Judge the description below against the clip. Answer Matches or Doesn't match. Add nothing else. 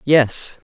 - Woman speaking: Matches